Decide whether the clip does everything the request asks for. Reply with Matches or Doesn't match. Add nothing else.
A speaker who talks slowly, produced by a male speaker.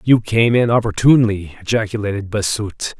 Matches